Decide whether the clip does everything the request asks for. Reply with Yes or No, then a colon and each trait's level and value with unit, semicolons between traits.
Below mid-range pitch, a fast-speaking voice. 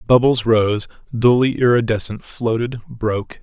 No: low, 115 Hz; slow, 105 wpm